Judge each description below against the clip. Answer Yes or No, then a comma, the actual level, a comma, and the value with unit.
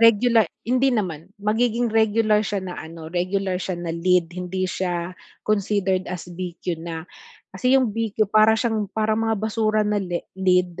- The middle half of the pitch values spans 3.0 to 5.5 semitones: Yes, average, 3.4 semitones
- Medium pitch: No, high, 195 Hz